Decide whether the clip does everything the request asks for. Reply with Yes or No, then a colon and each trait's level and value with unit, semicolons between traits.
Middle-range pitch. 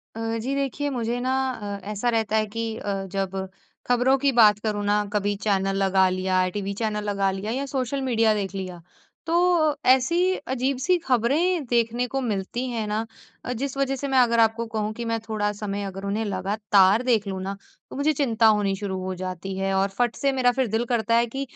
No: high, 225 Hz